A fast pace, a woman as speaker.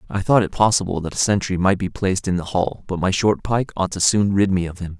No: fast, 290 wpm; male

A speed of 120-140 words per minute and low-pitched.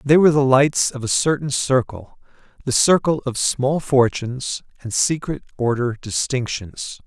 Yes: slow, 135 wpm; low, 130 Hz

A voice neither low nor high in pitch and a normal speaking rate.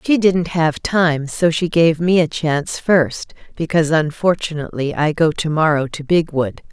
Yes: medium, 160 Hz; average, 170 wpm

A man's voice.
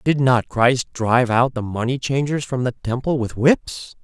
Yes: male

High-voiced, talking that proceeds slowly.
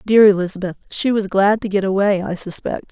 No: high, 195 Hz; fast, 205 wpm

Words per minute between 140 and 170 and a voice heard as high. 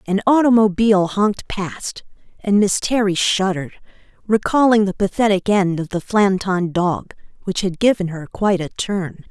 Yes: average, 150 wpm; high, 195 Hz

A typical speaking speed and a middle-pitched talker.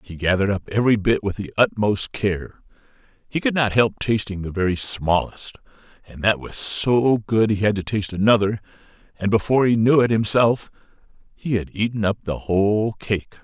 No: average, 180 wpm; low, 105 Hz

